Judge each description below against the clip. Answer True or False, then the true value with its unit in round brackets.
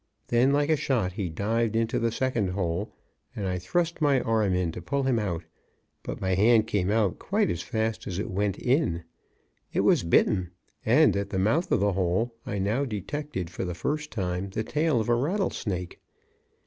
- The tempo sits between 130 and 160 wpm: False (195 wpm)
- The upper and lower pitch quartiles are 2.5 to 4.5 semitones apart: False (5.1 semitones)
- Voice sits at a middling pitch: False (105 Hz)